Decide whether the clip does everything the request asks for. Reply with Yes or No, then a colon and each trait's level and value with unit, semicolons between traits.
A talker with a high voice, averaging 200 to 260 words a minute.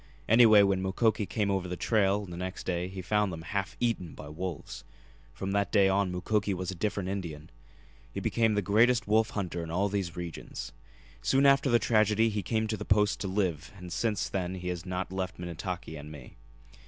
No: very low, 95 Hz; fast, 205 wpm